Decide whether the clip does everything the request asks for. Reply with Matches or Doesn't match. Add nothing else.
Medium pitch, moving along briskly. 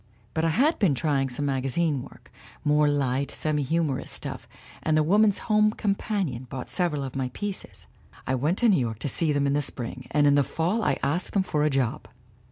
Matches